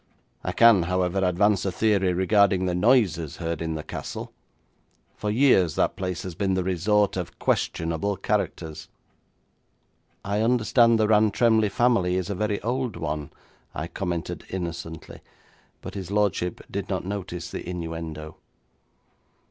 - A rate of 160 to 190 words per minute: No, average, 140 wpm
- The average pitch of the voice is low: Yes, very low, 95 Hz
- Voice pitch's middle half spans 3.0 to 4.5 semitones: Yes, average, 3.6 semitones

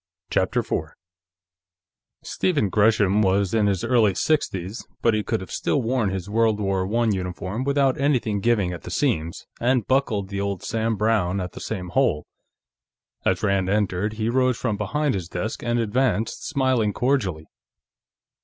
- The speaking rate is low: No, average, 160 wpm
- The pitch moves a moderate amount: Yes, average, 3.9 semitones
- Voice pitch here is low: Yes, low, 105 Hz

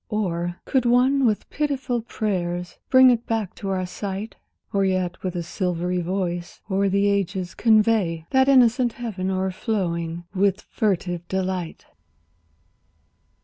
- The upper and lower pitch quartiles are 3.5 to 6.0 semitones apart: Yes, average, 4.1 semitones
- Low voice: No, high, 195 Hz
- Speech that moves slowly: Yes, slow, 130 wpm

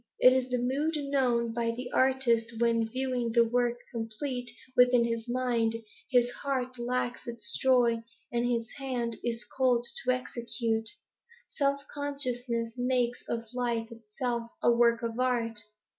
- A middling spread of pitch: No, narrow, 1.6 semitones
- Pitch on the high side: Yes, high, 240 Hz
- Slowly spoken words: No, average, 145 wpm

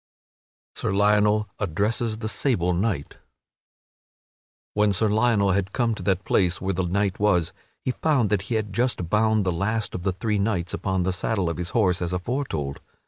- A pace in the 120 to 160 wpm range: No, average, 185 wpm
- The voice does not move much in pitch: No, average, 3.1 semitones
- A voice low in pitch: Yes, low, 100 Hz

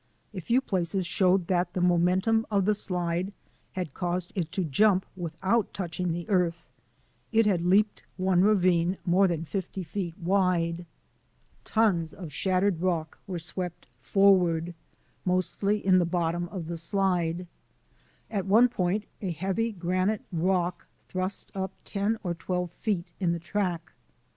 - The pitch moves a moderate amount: No, narrow, 2.3 semitones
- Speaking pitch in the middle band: Yes, medium, 180 Hz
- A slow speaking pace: No, average, 145 wpm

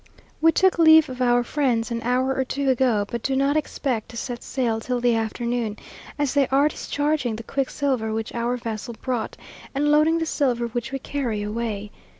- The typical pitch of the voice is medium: No, very high, 250 Hz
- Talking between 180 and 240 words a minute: Yes, average, 190 wpm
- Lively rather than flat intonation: No, average, 3.3 semitones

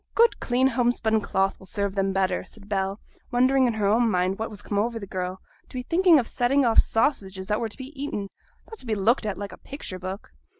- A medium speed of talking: No, fast, 245 wpm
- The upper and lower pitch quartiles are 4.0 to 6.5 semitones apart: Yes, average, 4.3 semitones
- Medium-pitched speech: No, high, 220 Hz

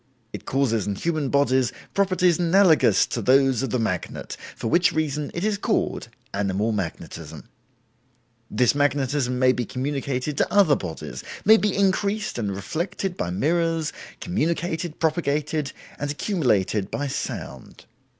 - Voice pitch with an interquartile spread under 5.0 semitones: No, wide, 5.4 semitones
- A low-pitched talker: No, medium, 145 Hz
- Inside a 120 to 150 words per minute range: Yes, slow, 135 wpm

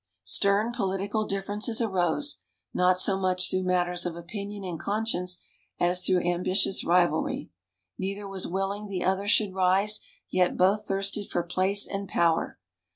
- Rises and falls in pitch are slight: Yes, narrow, 1.9 semitones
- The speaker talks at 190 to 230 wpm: No, average, 145 wpm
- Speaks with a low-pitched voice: No, high, 190 Hz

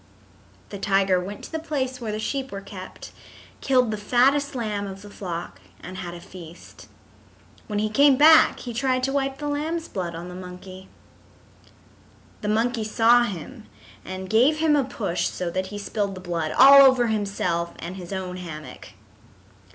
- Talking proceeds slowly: No, average, 175 wpm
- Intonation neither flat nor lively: No, wide, 5.9 semitones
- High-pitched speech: Yes, high, 205 Hz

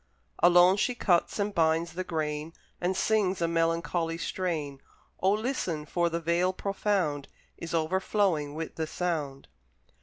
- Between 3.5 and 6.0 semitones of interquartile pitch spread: No, average, 2.8 semitones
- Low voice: No, medium, 170 Hz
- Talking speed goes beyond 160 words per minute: No, average, 140 wpm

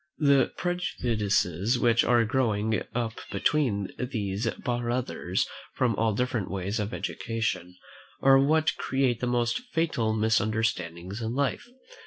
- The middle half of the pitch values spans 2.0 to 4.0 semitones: Yes, average, 3.3 semitones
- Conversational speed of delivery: No, slow, 120 wpm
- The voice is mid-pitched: No, low, 115 Hz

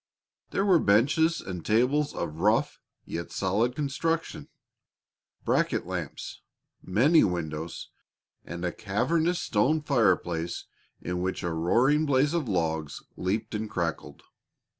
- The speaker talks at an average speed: No, slow, 120 wpm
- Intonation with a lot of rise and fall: Yes, wide, 9.0 semitones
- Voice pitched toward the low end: Yes, low, 105 Hz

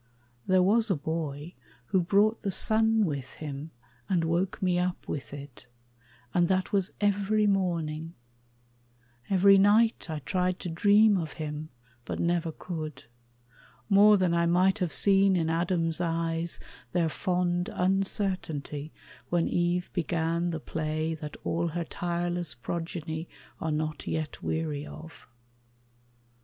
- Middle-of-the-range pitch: Yes, medium, 175 Hz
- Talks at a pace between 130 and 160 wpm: Yes, slow, 135 wpm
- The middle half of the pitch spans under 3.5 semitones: Yes, average, 2.9 semitones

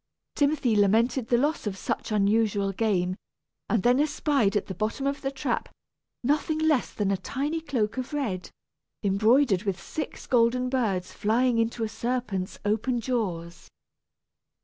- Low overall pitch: No, high, 230 Hz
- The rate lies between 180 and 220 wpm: No, average, 150 wpm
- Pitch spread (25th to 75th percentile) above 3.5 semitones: Yes, average, 4.7 semitones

